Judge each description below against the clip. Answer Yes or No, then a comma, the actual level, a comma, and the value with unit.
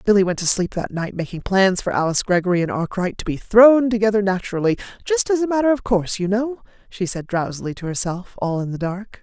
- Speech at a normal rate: No, fast, 220 wpm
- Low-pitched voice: No, high, 200 Hz